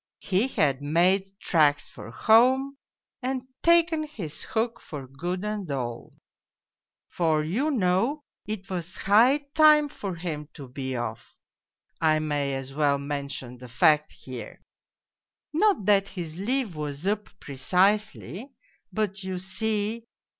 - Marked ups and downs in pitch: Yes, wide, 7.3 semitones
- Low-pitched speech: No, medium, 185 Hz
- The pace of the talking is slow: Yes, slow, 130 wpm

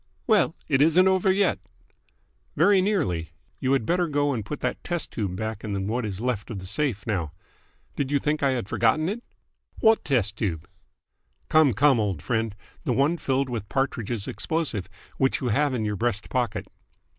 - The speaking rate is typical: Yes, average, 180 wpm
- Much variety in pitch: Yes, wide, 6.2 semitones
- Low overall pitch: Yes, low, 125 Hz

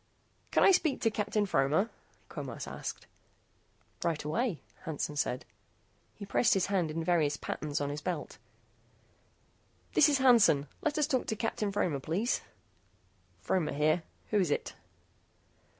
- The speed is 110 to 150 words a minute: Yes, average, 140 wpm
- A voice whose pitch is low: No, medium, 180 Hz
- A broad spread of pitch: Yes, wide, 6.7 semitones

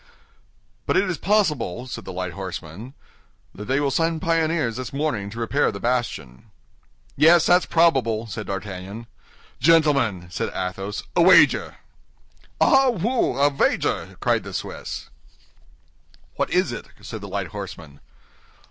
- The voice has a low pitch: Yes, low, 120 Hz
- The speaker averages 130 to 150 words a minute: Yes, average, 140 wpm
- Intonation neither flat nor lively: No, wide, 8.3 semitones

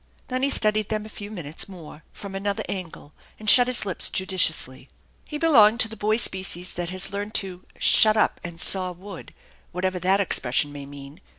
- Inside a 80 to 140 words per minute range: No, average, 190 wpm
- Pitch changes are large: No, average, 3.7 semitones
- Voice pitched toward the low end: No, high, 190 Hz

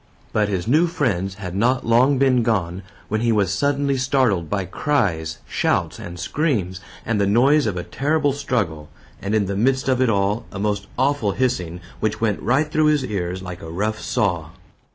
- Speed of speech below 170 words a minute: No, average, 190 wpm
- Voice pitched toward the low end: Yes, low, 110 Hz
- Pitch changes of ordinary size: No, wide, 5.8 semitones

